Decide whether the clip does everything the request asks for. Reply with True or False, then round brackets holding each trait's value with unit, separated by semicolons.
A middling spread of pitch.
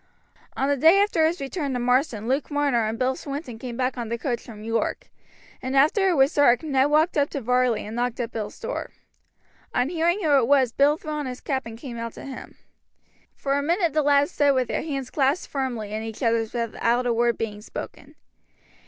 True (3.7 semitones)